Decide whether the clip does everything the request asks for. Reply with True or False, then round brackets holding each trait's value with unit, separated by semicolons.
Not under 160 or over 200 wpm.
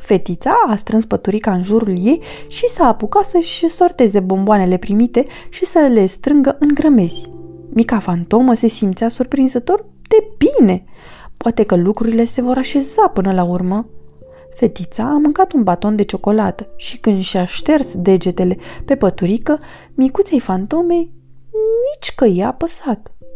False (145 wpm)